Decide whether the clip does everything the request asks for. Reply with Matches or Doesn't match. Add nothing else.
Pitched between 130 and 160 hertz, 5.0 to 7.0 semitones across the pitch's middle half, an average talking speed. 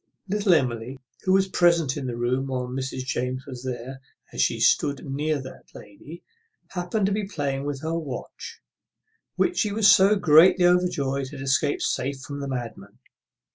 Matches